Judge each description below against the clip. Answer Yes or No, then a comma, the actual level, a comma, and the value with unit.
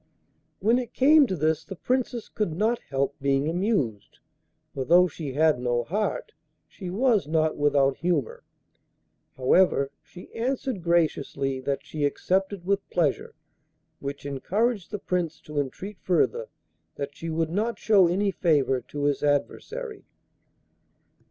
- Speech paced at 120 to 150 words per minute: Yes, average, 140 wpm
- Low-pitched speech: No, medium, 170 Hz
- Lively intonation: Yes, wide, 6.5 semitones